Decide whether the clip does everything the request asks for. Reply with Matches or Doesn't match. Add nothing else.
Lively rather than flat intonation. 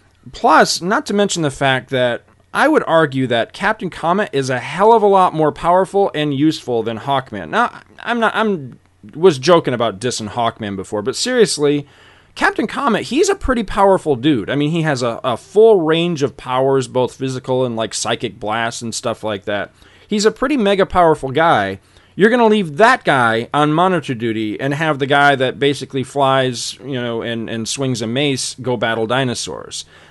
Matches